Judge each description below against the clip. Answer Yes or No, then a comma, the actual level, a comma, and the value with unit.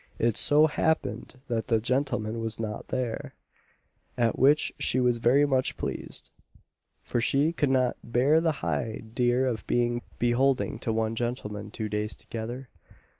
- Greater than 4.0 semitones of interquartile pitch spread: No, average, 2.8 semitones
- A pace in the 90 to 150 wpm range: Yes, average, 145 wpm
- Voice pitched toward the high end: No, low, 120 Hz